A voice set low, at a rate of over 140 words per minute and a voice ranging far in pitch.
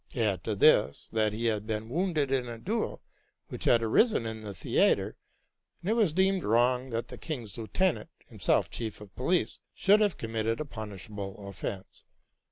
Yes: low, 115 Hz; average, 175 wpm; wide, 6.3 semitones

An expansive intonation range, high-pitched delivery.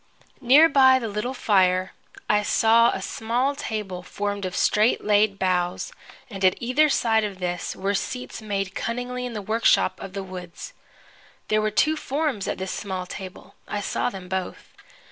No: average, 4.2 semitones; high, 210 Hz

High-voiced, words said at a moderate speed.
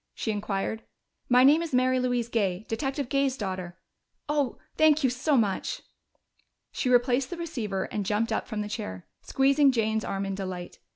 Yes: high, 240 Hz; average, 170 wpm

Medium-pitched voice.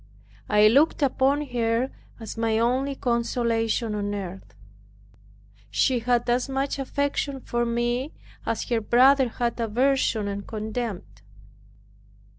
No: high, 235 Hz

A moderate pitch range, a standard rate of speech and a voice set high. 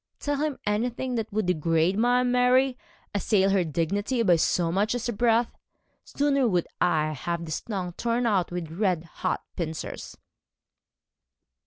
No: wide, 6.0 semitones; average, 150 wpm; high, 205 Hz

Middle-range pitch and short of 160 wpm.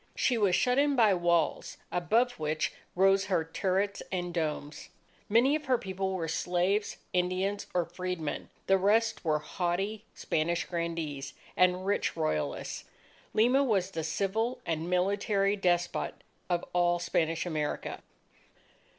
Yes: medium, 180 Hz; slow, 135 wpm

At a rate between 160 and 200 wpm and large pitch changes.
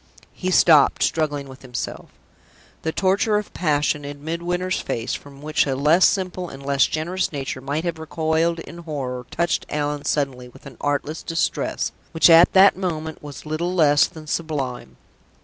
No: average, 165 wpm; average, 3.2 semitones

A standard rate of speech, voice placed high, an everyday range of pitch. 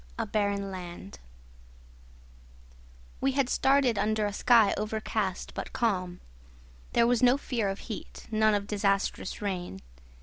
No: slow, 130 wpm; high, 210 Hz; average, 3.0 semitones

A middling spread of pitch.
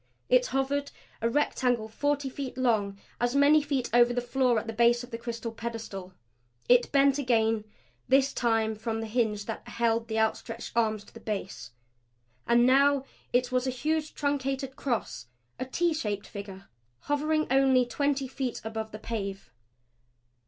Yes: average, 3.5 semitones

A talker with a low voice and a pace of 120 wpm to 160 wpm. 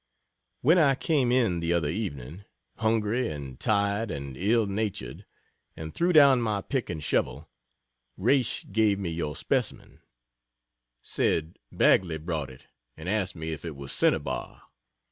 Yes: very low, 95 Hz; average, 145 wpm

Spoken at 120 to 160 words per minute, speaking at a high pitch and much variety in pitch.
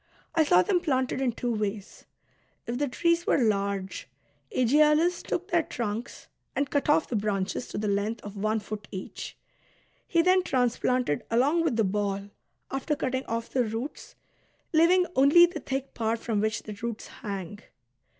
No: average, 170 wpm; high, 240 Hz; wide, 6.0 semitones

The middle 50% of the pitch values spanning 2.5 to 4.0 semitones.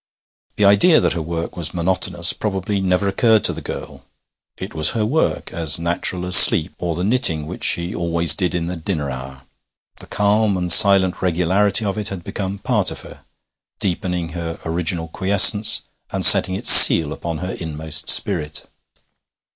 Yes: average, 3.0 semitones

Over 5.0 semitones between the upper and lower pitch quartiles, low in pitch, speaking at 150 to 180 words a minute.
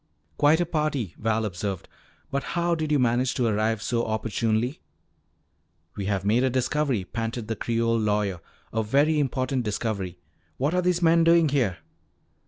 Yes: wide, 5.4 semitones; low, 120 Hz; average, 160 wpm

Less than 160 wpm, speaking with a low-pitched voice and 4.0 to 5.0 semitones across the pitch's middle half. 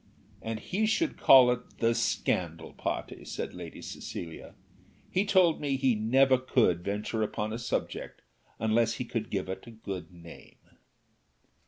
Yes: average, 150 wpm; low, 115 Hz; average, 4.4 semitones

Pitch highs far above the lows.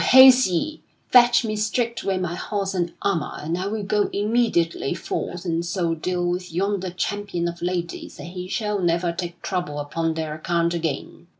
No: average, 3.2 semitones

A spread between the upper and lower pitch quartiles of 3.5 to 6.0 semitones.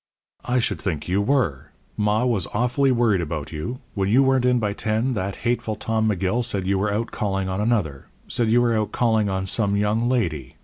Yes: average, 3.9 semitones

